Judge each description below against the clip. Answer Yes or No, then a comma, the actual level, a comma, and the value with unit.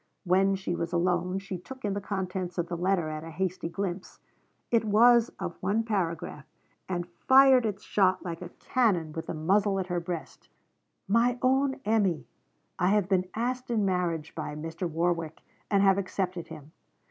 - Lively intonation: No, average, 3.3 semitones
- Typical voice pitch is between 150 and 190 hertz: Yes, medium, 185 Hz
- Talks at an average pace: Yes, average, 175 wpm